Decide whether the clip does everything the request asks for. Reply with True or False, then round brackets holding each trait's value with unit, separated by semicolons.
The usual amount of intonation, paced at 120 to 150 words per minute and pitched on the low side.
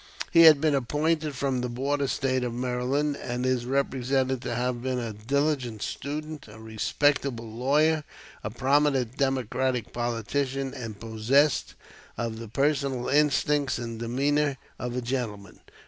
True (3.0 semitones; 140 wpm; 130 Hz)